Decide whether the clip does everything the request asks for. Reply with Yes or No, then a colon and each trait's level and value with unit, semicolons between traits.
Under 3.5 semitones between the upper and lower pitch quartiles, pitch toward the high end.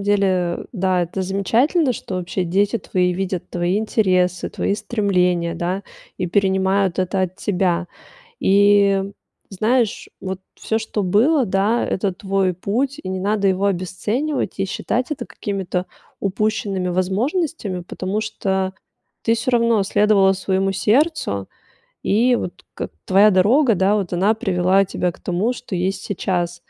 Yes: average, 2.7 semitones; high, 195 Hz